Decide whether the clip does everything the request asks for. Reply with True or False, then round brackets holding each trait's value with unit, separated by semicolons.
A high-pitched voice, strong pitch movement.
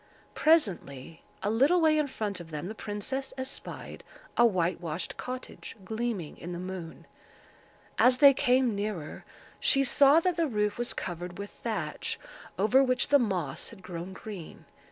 True (210 Hz; 6.8 semitones)